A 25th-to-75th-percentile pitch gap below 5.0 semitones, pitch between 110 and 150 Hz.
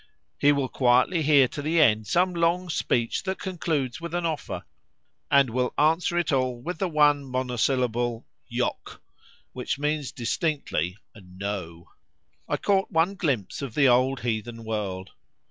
No: wide, 5.5 semitones; low, 135 Hz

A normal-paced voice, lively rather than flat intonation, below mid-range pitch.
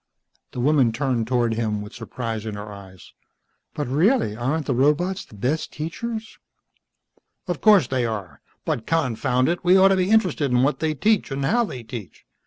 Yes: average, 185 wpm; wide, 7.2 semitones; low, 130 Hz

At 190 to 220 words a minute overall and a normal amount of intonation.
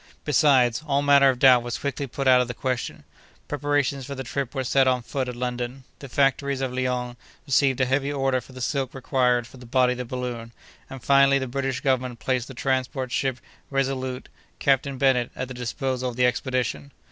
No: fast, 205 wpm; narrow, 1.7 semitones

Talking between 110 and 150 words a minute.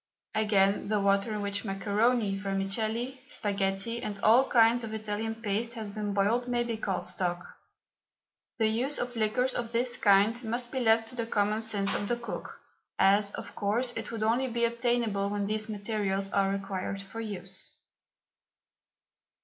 No: average, 165 wpm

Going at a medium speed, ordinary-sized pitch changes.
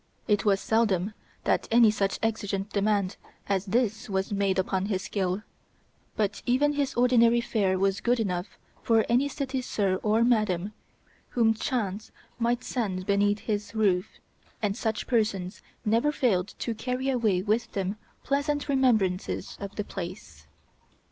Yes: average, 145 wpm; average, 3.4 semitones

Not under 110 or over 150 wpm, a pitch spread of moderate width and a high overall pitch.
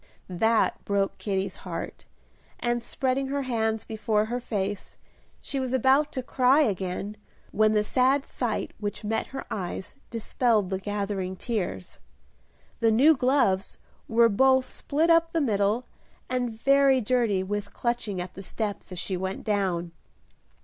Yes: average, 145 wpm; average, 4.4 semitones; high, 220 Hz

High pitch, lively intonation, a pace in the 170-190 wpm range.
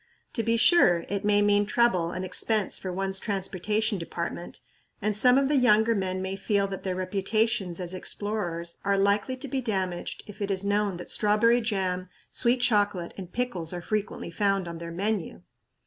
No: high, 200 Hz; average, 2.9 semitones; average, 180 wpm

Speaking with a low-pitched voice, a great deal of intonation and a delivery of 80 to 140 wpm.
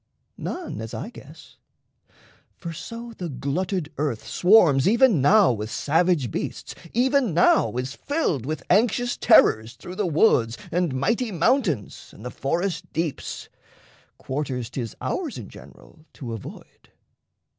No: medium, 165 Hz; wide, 8.4 semitones; slow, 135 wpm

